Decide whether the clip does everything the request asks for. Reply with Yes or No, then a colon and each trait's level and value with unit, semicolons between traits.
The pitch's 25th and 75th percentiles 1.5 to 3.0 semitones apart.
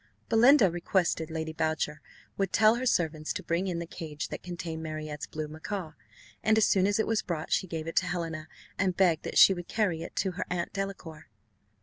No: average, 3.5 semitones